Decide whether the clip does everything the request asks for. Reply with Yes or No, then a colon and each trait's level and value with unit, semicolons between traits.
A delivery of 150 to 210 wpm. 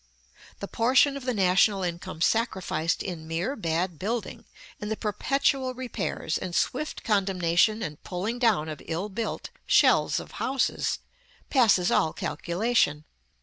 No: slow, 135 wpm